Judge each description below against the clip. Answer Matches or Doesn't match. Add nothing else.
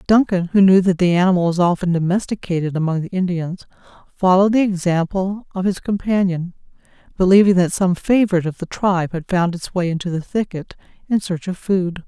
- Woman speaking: Matches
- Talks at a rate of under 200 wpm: Matches